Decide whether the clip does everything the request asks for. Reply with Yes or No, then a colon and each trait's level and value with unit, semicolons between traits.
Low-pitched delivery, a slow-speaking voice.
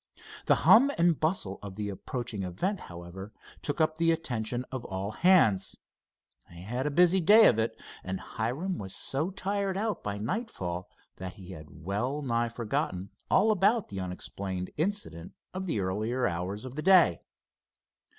No: low, 120 Hz; average, 160 wpm